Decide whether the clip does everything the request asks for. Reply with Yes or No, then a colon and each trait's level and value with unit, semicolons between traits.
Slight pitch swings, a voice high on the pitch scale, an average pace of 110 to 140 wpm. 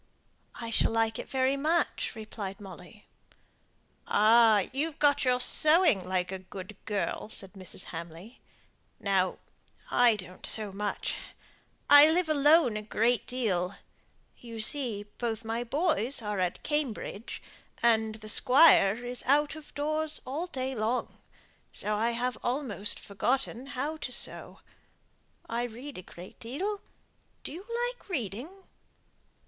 No: wide, 5.5 semitones; high, 235 Hz; slow, 135 wpm